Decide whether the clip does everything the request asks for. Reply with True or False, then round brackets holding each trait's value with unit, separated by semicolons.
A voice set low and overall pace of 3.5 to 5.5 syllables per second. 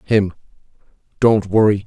True (105 Hz; 4.3 syllables/s)